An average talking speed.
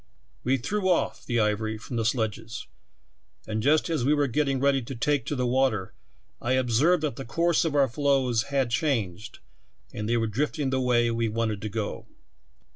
Yes: average, 190 wpm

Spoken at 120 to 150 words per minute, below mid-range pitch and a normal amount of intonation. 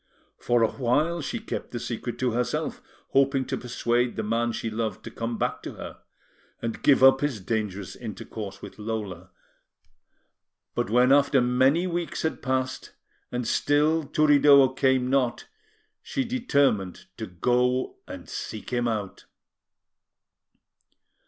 Yes: average, 140 wpm; low, 125 Hz; average, 3.7 semitones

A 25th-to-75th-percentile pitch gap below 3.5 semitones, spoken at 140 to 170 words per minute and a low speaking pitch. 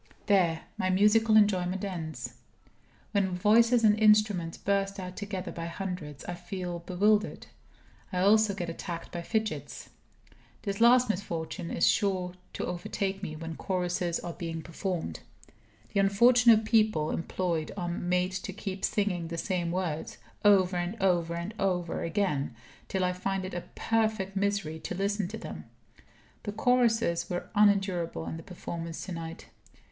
No: average, 3.0 semitones; average, 150 wpm; medium, 185 Hz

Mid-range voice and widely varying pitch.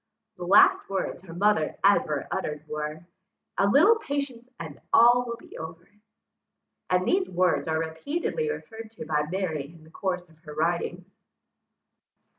Yes: medium, 180 Hz; wide, 6.1 semitones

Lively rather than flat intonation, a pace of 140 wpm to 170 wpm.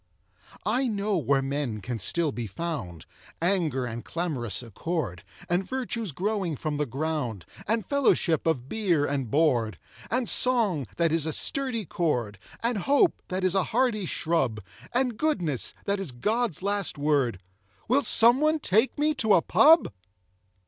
Yes: wide, 8.4 semitones; average, 150 wpm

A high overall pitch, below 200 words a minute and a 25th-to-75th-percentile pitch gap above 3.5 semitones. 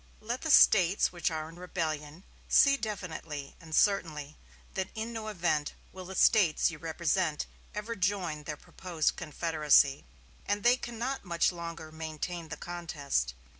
No: medium, 170 Hz; average, 145 wpm; average, 4.4 semitones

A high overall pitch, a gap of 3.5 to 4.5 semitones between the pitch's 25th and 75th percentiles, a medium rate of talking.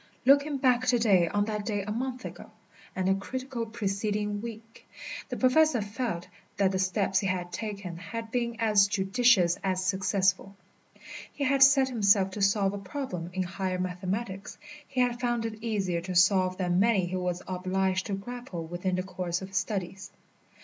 Yes: high, 200 Hz; average, 3.9 semitones; average, 180 wpm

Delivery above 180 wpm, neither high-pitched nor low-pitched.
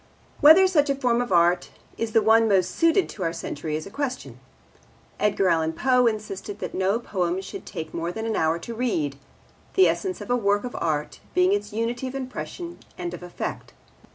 No: average, 200 wpm; high, 210 Hz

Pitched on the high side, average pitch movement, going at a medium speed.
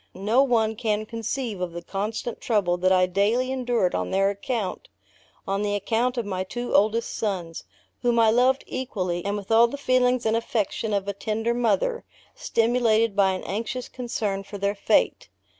Yes: high, 220 Hz; average, 3.4 semitones; average, 175 wpm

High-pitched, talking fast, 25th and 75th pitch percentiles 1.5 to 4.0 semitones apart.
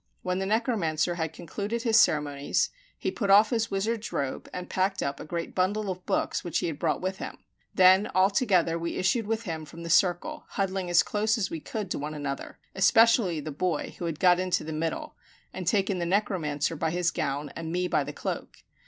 No: medium, 180 Hz; fast, 215 wpm; average, 3.7 semitones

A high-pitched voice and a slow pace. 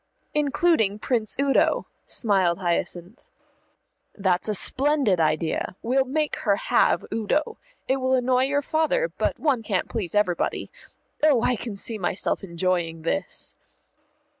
Yes: high, 225 Hz; slow, 130 wpm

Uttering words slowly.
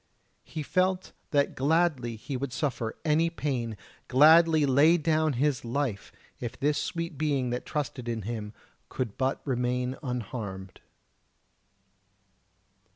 Yes: slow, 120 wpm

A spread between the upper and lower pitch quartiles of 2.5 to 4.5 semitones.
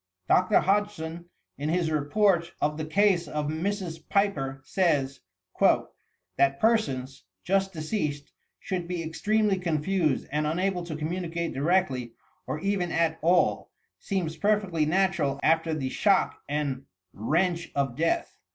Yes: average, 4.1 semitones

